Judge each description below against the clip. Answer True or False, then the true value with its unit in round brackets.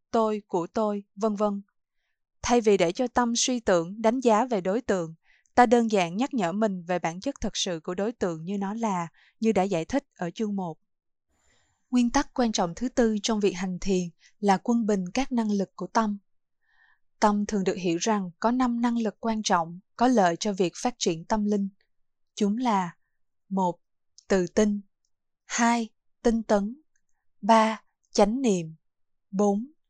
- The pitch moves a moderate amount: True (3.7 semitones)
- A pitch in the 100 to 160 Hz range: False (210 Hz)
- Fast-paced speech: False (180 wpm)